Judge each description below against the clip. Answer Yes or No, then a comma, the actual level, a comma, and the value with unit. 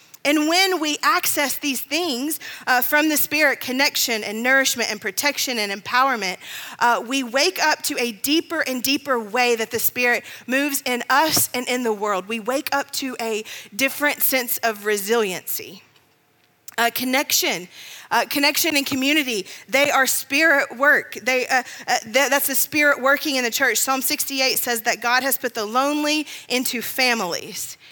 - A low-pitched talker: No, very high, 260 Hz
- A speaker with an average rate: Yes, average, 170 wpm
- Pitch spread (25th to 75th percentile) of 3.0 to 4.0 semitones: Yes, average, 3.3 semitones